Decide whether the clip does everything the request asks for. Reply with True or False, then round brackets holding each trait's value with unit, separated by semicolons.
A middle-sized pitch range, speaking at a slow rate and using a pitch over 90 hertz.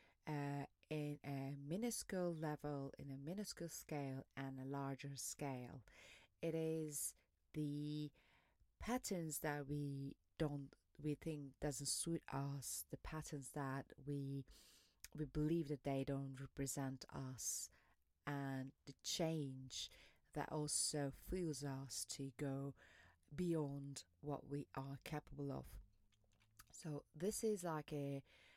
False (2.2 semitones; 120 wpm; 140 Hz)